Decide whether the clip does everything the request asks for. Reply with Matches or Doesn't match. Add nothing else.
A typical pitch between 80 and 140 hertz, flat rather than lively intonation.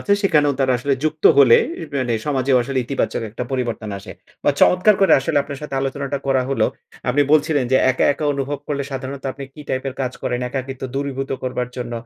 Matches